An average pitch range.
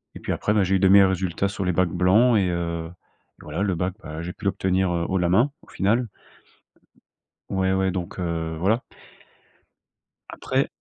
No: narrow, 2.2 semitones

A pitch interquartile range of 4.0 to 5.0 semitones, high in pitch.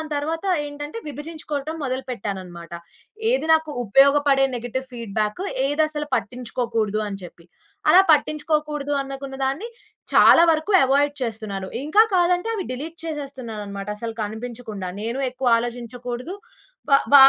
Yes: average, 4.7 semitones; very high, 270 Hz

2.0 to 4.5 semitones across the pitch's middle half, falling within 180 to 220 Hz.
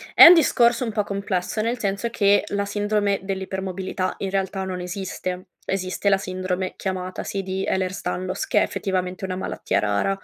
No: narrow, 1.5 semitones; high, 190 Hz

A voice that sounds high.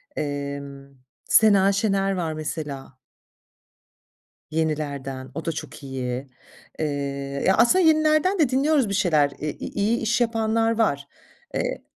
No: medium, 170 Hz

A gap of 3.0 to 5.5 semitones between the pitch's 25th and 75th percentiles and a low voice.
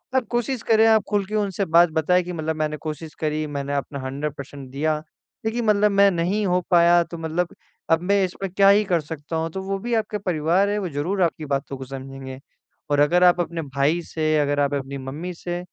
No: average, 5.0 semitones; medium, 170 Hz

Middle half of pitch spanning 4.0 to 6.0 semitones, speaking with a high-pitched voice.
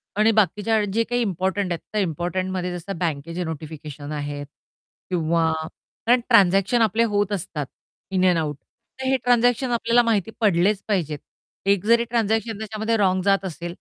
Yes: average, 4.7 semitones; high, 195 Hz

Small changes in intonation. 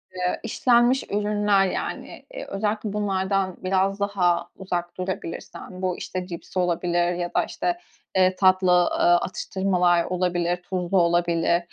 Yes: narrow, 2.0 semitones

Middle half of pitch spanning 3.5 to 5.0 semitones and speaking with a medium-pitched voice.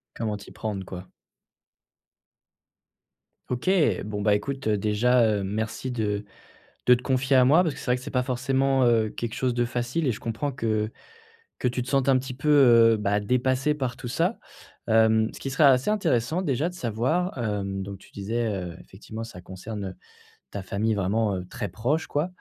No: average, 4.0 semitones; low, 120 Hz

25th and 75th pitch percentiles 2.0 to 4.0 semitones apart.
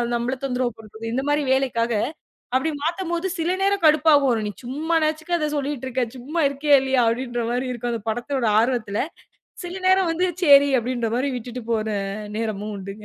No: average, 4.5 semitones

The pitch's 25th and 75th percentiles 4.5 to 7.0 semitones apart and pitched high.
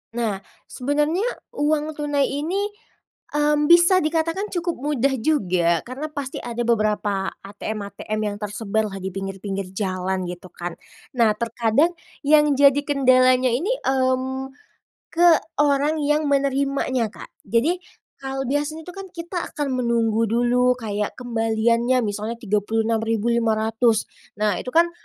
Yes: average, 5.2 semitones; very high, 250 Hz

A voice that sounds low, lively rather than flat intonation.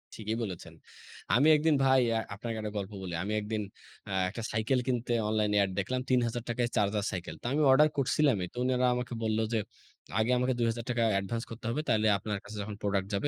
No: low, 115 Hz; average, 3.2 semitones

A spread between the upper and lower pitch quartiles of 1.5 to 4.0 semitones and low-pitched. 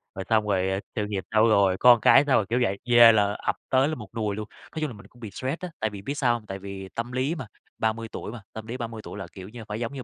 Yes: average, 3.2 semitones; low, 110 Hz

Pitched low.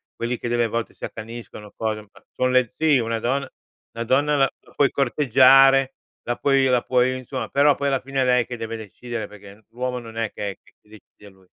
Yes: low, 125 Hz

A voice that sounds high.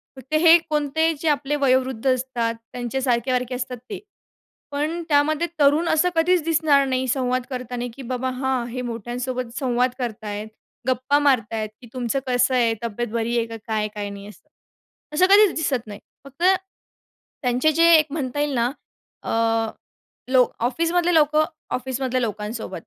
Yes: very high, 255 Hz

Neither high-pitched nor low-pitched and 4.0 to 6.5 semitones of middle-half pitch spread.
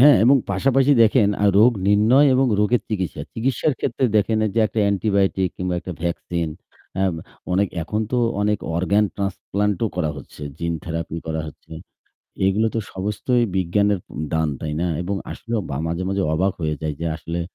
No: low, 100 Hz; average, 4.3 semitones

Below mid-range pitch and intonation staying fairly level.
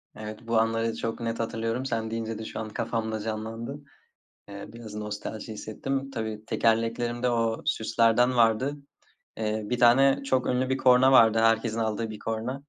Yes: low, 115 Hz; narrow, 1.7 semitones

